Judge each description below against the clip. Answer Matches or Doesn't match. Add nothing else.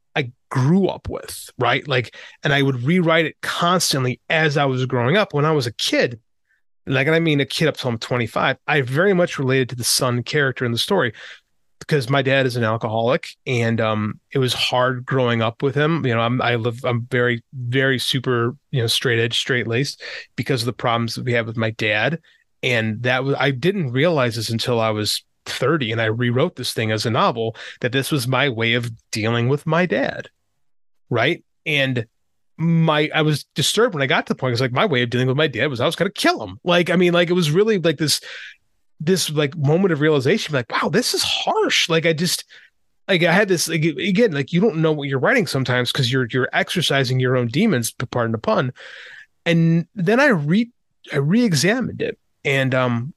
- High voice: Doesn't match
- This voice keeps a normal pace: Doesn't match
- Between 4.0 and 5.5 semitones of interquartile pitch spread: Matches